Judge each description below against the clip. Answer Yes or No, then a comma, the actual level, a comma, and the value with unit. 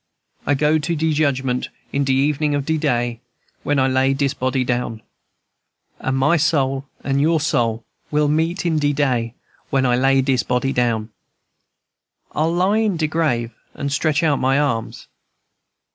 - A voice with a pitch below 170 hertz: Yes, medium, 140 Hz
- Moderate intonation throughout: Yes, average, 3.1 semitones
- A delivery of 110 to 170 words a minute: Yes, average, 165 wpm